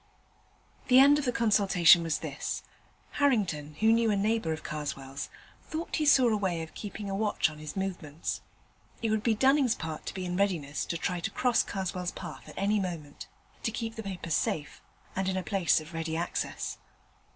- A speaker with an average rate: Yes, average, 195 wpm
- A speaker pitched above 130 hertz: Yes, high, 190 Hz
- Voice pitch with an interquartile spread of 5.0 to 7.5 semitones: Yes, wide, 5.5 semitones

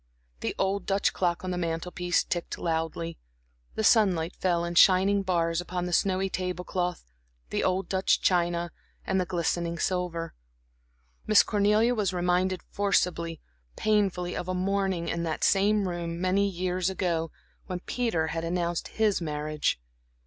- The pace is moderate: Yes, average, 150 wpm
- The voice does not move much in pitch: Yes, narrow, 2.2 semitones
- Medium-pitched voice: Yes, medium, 180 Hz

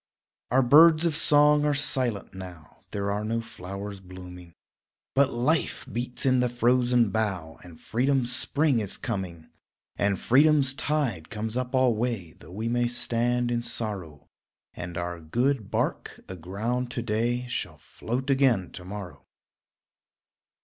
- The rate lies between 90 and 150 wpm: Yes, average, 140 wpm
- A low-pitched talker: Yes, low, 120 Hz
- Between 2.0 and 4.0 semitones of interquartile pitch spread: No, average, 5.0 semitones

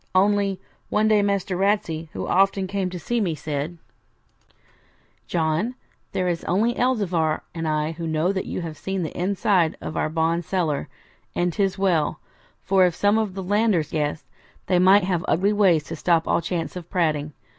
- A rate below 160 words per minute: No, average, 175 wpm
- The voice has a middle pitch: Yes, medium, 180 Hz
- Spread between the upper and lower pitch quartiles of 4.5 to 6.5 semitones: No, average, 3.5 semitones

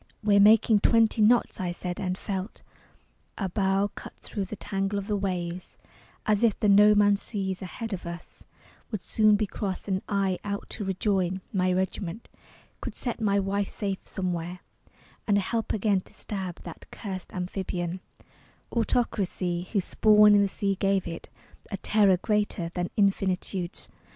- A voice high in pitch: Yes, high, 195 Hz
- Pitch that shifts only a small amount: Yes, narrow, 2.2 semitones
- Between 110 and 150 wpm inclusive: No, average, 160 wpm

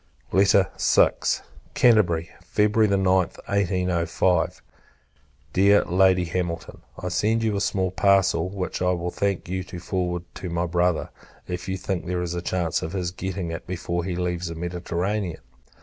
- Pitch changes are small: Yes, narrow, 1.8 semitones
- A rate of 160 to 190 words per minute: No, average, 150 wpm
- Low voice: Yes, very low, 90 Hz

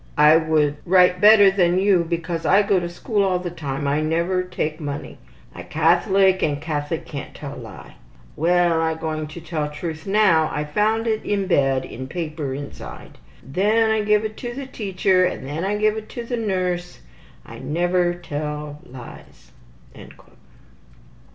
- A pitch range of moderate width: Yes, average, 4.4 semitones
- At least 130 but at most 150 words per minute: No, average, 165 wpm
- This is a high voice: No, medium, 175 Hz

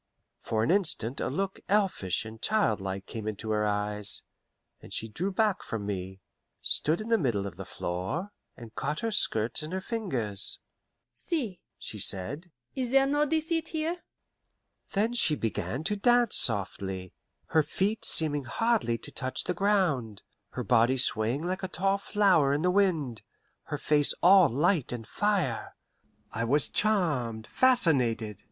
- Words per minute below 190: Yes, average, 155 wpm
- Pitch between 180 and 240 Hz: No, medium, 150 Hz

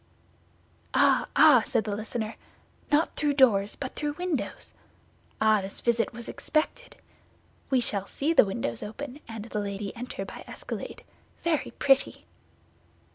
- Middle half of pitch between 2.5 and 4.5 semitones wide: No, wide, 5.5 semitones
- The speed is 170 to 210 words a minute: No, slow, 135 wpm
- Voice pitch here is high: Yes, high, 235 Hz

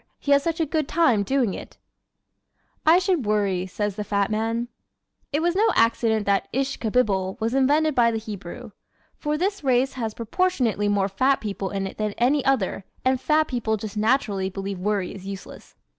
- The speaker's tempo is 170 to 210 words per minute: Yes, average, 190 wpm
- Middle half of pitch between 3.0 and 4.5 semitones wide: No, wide, 5.4 semitones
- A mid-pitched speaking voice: No, high, 225 Hz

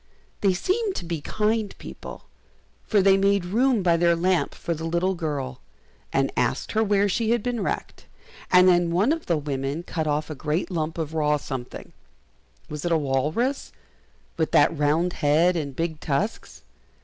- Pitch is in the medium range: Yes, medium, 170 Hz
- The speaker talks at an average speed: Yes, average, 175 wpm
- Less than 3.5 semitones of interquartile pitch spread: No, average, 4.7 semitones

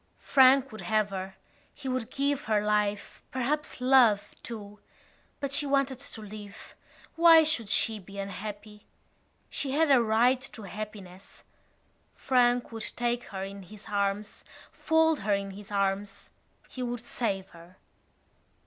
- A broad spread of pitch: No, average, 4.5 semitones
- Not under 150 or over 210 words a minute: No, average, 140 wpm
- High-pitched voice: Yes, high, 220 Hz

